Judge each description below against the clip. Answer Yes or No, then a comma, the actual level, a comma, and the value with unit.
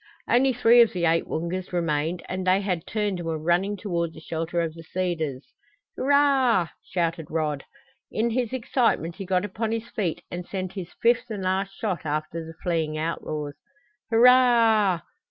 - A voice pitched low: No, medium, 185 Hz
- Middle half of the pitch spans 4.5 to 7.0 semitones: Yes, average, 5.2 semitones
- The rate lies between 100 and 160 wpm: No, average, 170 wpm